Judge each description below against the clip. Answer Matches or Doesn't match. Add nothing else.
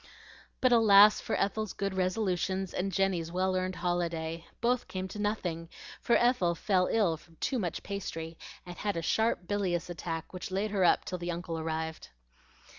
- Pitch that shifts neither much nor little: Matches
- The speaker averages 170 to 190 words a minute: Matches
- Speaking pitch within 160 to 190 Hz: Matches